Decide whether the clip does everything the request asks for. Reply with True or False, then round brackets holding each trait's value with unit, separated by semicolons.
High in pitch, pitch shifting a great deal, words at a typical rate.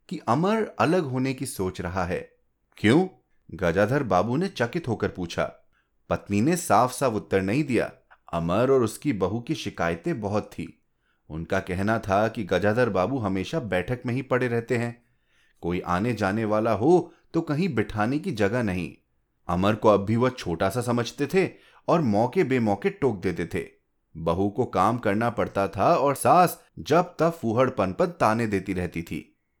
False (110 Hz; 5.8 semitones; 170 wpm)